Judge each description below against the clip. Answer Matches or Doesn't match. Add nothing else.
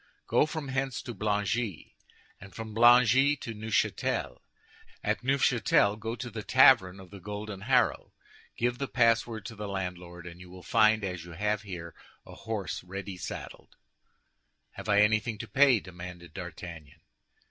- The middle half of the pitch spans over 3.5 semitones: Matches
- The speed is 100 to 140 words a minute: Doesn't match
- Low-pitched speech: Matches